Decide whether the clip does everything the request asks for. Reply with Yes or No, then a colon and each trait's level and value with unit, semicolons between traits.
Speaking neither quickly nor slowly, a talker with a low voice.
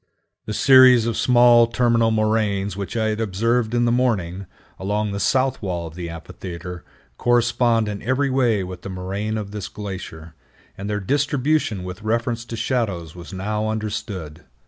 Yes: average, 165 wpm; low, 110 Hz